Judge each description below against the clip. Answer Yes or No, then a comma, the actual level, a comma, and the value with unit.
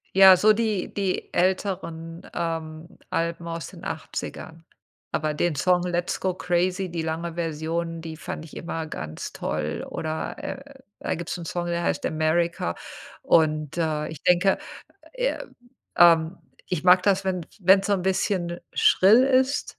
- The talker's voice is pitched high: No, medium, 170 Hz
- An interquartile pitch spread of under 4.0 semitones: Yes, average, 2.7 semitones